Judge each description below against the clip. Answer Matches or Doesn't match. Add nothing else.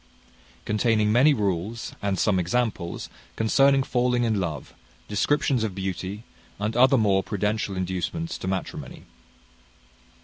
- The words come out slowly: Matches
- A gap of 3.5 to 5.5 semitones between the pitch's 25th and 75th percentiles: Matches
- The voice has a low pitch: Matches